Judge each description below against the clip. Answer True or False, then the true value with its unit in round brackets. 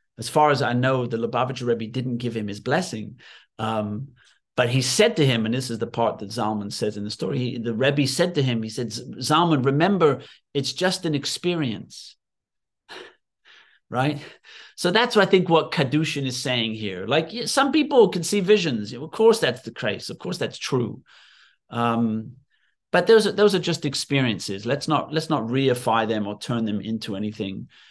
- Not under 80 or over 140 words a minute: False (190 wpm)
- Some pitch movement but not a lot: False (5.8 semitones)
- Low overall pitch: True (130 Hz)